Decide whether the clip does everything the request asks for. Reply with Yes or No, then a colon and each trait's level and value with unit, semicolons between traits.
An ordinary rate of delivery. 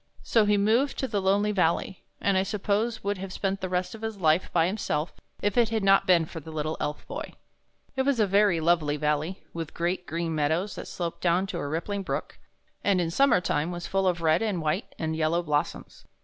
No: fast, 220 wpm